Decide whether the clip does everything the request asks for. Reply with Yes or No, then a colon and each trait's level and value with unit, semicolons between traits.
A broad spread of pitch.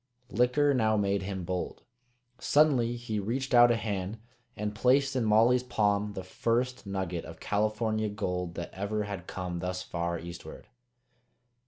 No: average, 4.3 semitones